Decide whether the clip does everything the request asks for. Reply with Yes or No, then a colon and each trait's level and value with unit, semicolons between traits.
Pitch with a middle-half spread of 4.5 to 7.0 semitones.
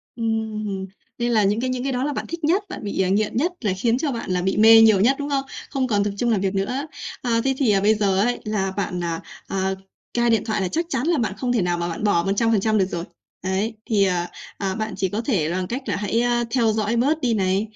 No: average, 3.9 semitones